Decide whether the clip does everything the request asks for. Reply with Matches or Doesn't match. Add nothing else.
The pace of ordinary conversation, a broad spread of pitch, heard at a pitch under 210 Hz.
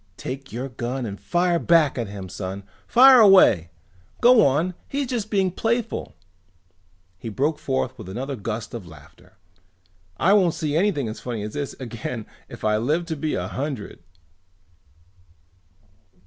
Matches